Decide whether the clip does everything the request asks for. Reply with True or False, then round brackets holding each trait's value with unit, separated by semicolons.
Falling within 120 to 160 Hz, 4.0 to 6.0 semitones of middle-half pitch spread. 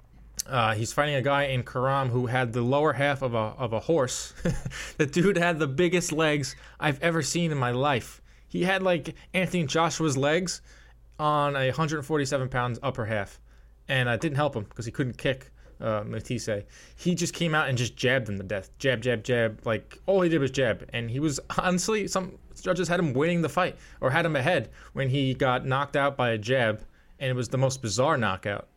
True (135 Hz; 5.1 semitones)